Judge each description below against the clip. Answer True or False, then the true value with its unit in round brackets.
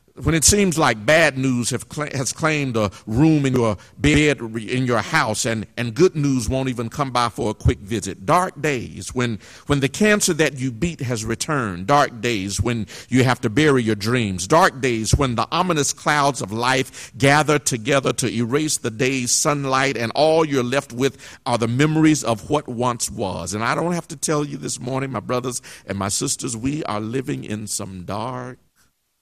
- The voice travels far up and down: False (4.1 semitones)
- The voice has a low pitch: True (130 Hz)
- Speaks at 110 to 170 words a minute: False (200 wpm)